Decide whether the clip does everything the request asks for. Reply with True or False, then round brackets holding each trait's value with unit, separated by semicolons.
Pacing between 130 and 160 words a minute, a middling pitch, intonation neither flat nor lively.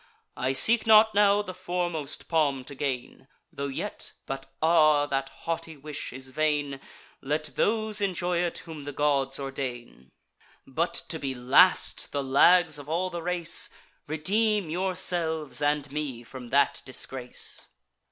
True (140 wpm; 150 Hz; 4.5 semitones)